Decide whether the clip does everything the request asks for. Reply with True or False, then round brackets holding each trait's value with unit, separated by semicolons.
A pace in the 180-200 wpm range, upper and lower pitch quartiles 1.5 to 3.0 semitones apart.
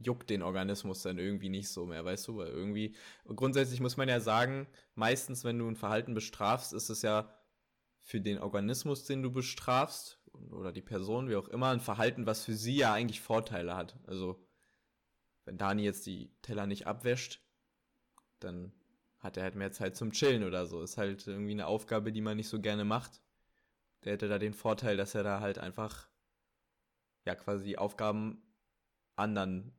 True (185 wpm; 2.7 semitones)